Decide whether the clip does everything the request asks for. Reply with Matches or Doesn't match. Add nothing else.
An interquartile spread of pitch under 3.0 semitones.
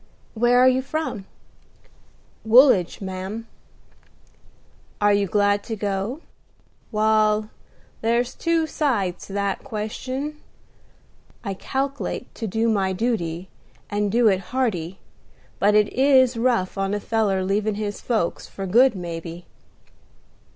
Doesn't match